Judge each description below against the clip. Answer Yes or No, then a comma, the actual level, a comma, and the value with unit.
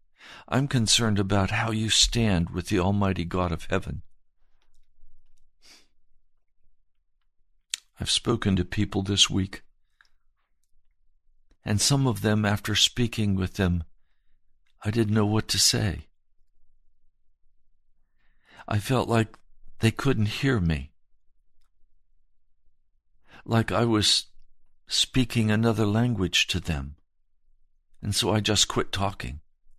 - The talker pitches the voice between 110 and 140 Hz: No, low, 100 Hz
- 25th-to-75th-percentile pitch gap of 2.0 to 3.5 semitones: No, average, 4.2 semitones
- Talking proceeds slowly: Yes, slow, 105 wpm